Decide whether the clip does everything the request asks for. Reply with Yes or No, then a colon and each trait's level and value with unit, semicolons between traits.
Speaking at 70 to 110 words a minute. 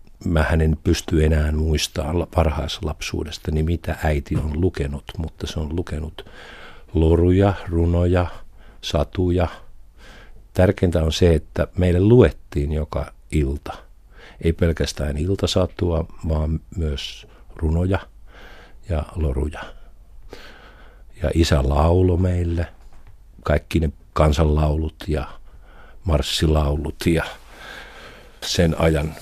Yes: average, 100 wpm